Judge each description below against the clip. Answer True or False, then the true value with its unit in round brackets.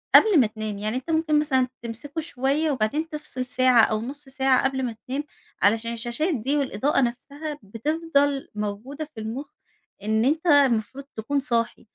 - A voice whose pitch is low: False (265 Hz)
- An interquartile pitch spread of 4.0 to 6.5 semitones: True (4.3 semitones)